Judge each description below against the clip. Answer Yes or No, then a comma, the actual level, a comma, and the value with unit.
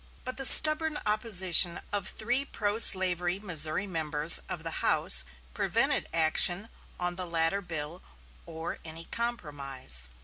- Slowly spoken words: Yes, slow, 130 wpm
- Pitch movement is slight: No, average, 4.7 semitones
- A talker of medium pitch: Yes, medium, 175 Hz